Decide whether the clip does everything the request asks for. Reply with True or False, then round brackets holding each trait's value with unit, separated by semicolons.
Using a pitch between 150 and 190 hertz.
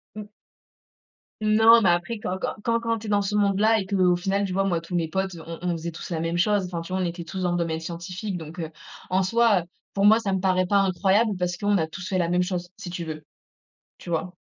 True (185 Hz)